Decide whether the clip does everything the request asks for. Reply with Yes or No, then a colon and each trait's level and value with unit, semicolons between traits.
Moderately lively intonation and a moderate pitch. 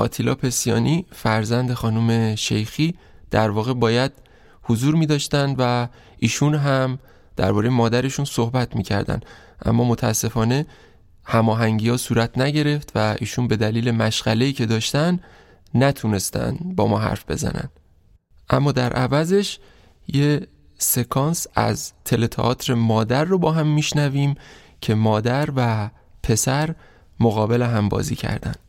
No: average, 4.1 semitones; low, 120 Hz